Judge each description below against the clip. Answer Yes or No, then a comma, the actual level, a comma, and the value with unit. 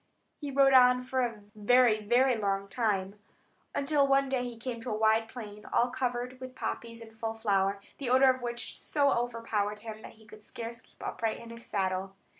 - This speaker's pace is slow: No, average, 200 wpm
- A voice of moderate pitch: No, high, 230 Hz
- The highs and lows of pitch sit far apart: No, average, 2.9 semitones